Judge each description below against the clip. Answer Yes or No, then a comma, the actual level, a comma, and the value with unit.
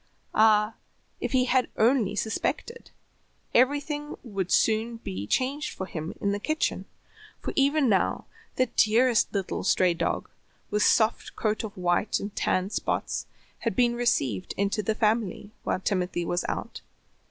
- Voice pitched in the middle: No, high, 215 Hz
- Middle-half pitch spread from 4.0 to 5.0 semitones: Yes, average, 4.5 semitones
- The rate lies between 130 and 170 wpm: Yes, average, 145 wpm